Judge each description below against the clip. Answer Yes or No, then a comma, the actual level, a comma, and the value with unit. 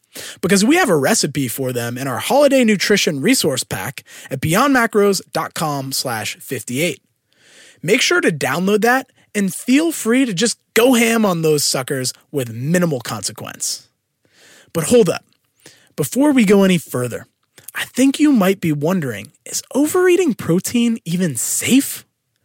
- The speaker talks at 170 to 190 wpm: No, average, 145 wpm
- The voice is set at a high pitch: Yes, high, 200 Hz